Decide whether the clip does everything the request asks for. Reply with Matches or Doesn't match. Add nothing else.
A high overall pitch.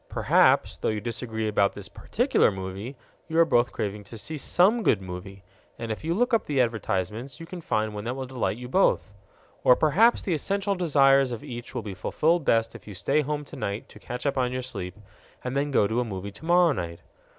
Doesn't match